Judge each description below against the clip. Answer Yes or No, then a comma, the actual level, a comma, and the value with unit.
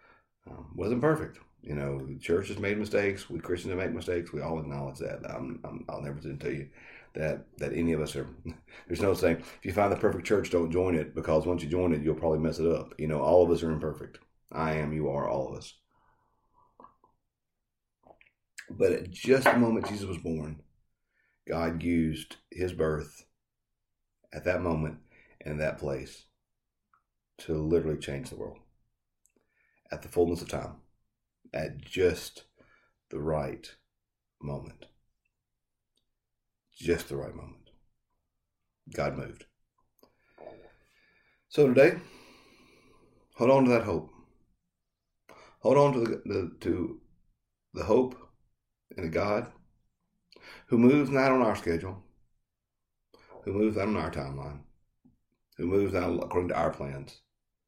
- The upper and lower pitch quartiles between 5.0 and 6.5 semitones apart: Yes, wide, 5.5 semitones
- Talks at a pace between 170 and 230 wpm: No, average, 145 wpm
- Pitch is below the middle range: Yes, very low, 85 Hz